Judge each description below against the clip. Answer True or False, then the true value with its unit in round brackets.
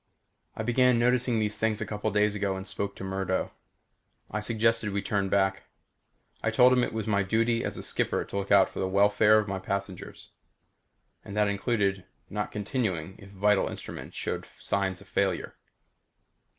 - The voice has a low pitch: True (105 Hz)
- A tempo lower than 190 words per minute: True (180 wpm)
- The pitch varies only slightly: True (2.2 semitones)